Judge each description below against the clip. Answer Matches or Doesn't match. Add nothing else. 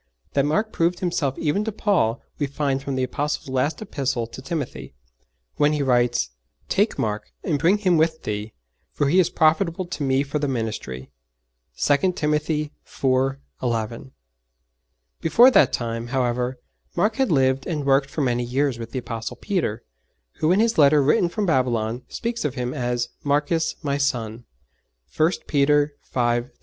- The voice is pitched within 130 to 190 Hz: Matches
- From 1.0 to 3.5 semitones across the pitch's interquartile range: Doesn't match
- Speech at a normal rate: Matches